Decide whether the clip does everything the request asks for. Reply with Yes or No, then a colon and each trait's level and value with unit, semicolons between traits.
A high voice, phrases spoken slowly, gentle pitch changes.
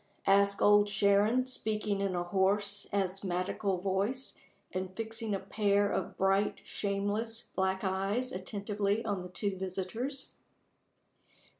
Yes: high, 200 Hz; slow, 120 wpm; narrow, 1.7 semitones